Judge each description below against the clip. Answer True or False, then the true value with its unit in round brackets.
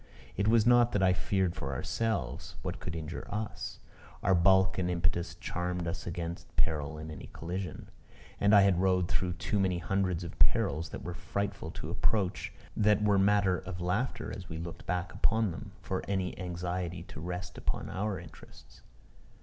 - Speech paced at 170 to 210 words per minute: True (175 wpm)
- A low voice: True (90 Hz)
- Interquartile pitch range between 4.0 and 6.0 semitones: False (2.5 semitones)